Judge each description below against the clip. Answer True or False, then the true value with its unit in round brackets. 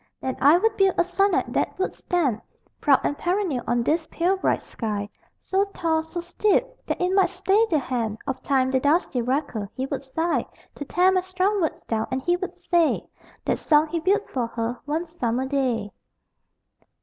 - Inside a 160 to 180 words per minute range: False (190 wpm)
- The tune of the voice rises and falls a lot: True (5.8 semitones)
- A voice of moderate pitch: False (315 Hz)